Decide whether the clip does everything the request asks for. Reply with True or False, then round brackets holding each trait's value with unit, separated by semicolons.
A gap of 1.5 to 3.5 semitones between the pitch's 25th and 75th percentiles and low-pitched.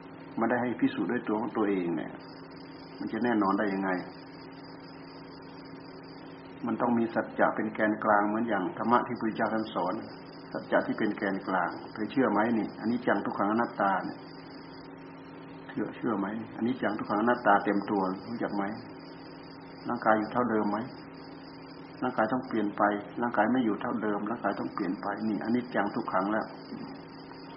True (2.9 semitones; 110 Hz)